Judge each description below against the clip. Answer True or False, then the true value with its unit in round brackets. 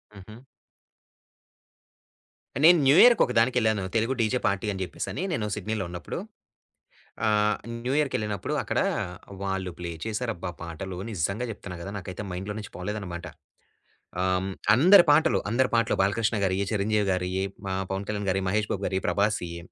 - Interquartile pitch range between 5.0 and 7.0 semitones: False (3.0 semitones)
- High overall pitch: False (100 Hz)